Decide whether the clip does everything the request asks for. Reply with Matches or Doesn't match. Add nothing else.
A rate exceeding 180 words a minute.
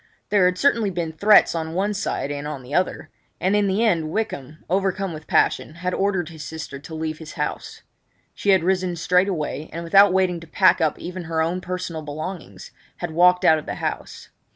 Matches